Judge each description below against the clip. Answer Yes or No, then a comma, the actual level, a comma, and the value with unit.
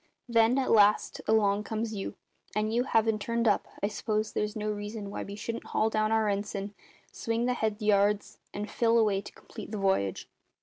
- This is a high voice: Yes, high, 215 Hz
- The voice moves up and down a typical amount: No, narrow, 1.5 semitones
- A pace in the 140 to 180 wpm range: No, average, 190 wpm